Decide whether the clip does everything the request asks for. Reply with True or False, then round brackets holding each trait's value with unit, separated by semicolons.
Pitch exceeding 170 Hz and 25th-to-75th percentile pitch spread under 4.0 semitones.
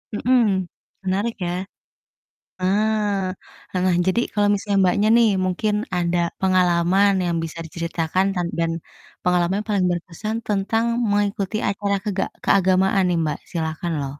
True (190 Hz; 2.8 semitones)